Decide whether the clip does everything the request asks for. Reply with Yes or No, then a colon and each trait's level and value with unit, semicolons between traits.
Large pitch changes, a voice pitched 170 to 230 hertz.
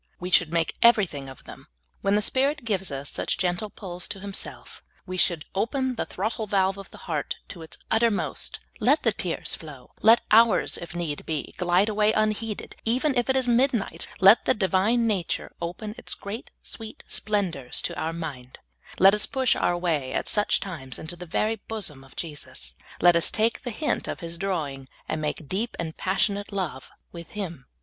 No: average, 4.8 semitones; high, 190 Hz